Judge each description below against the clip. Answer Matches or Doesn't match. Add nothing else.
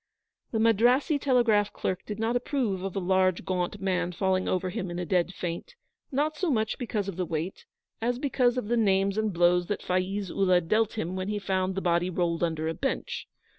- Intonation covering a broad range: Doesn't match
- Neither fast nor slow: Doesn't match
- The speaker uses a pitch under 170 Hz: Doesn't match